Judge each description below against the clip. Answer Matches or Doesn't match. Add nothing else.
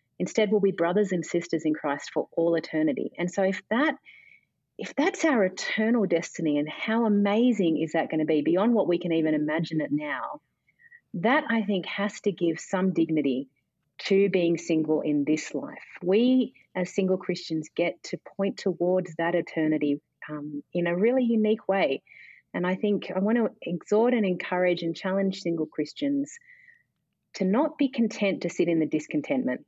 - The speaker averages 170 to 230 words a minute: Matches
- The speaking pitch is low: Doesn't match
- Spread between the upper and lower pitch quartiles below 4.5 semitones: Doesn't match